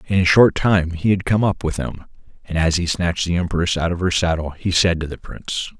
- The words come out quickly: Yes, fast, 260 wpm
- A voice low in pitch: Yes, very low, 85 Hz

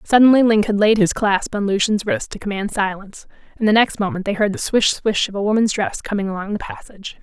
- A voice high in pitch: Yes, high, 210 Hz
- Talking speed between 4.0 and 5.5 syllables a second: No, 6.0 syllables/s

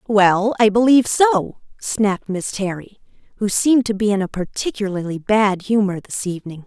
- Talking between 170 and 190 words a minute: No, average, 160 wpm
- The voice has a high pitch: Yes, high, 205 Hz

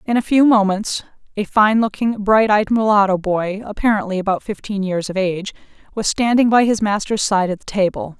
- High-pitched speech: Yes, high, 205 Hz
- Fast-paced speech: No, average, 190 wpm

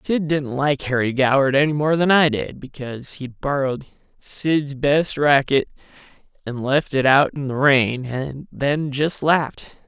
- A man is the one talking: Yes, male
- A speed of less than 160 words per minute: No, average, 165 wpm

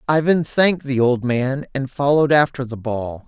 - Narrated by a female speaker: No, male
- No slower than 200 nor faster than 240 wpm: No, average, 185 wpm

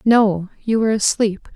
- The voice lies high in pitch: Yes, high, 210 Hz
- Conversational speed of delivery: Yes, average, 155 wpm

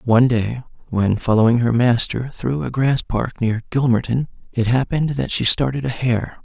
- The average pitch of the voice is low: Yes, low, 120 Hz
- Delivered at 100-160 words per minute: No, average, 175 wpm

